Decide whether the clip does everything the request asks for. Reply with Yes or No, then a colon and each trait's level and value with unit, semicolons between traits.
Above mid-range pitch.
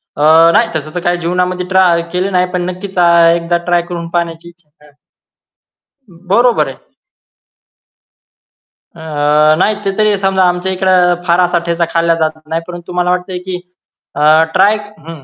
No: medium, 175 Hz